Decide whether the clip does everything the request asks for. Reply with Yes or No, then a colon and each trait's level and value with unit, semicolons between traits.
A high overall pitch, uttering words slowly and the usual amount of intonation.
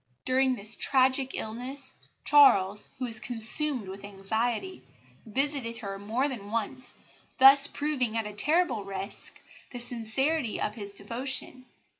Yes: high, 240 Hz; slow, 130 wpm; average, 4.2 semitones